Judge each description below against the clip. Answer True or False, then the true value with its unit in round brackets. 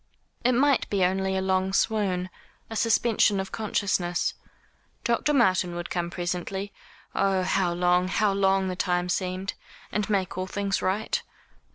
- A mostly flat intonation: True (1.9 semitones)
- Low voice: False (190 Hz)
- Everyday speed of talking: True (150 wpm)